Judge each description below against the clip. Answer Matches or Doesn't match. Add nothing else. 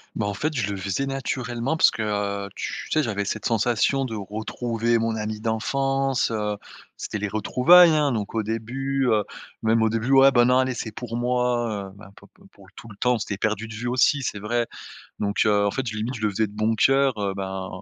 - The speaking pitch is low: Matches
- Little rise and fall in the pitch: Doesn't match